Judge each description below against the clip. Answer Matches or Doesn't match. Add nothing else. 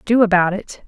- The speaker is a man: Doesn't match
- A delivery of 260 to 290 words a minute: Doesn't match